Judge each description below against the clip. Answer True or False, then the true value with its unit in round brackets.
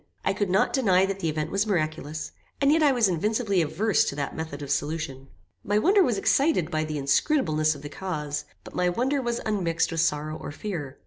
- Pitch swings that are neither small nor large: False (5.8 semitones)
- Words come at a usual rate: False (210 wpm)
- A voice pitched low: False (175 Hz)